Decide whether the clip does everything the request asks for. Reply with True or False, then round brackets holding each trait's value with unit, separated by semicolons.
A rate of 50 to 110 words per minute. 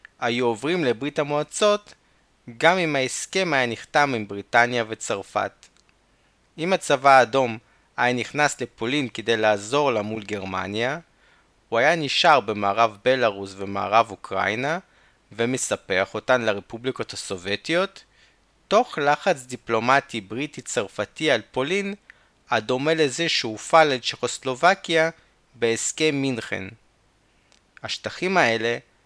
True (100 wpm)